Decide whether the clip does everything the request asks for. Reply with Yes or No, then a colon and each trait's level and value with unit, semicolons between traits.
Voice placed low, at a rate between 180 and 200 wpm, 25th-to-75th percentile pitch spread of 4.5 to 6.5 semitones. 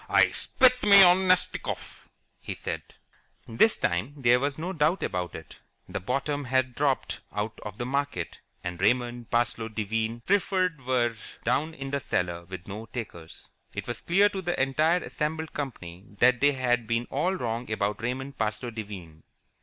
No: low, 125 Hz; average, 165 wpm; average, 5.3 semitones